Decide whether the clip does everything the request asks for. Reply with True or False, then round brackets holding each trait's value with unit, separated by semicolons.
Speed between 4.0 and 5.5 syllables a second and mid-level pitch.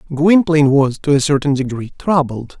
True (5.4 syllables/s; 145 Hz)